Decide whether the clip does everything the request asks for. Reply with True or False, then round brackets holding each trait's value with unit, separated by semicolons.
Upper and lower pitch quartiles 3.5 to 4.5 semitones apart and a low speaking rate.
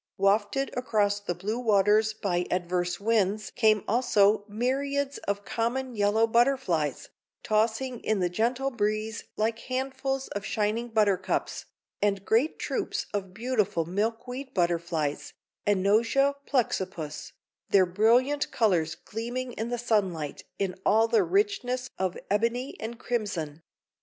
True (4.0 semitones; 120 wpm)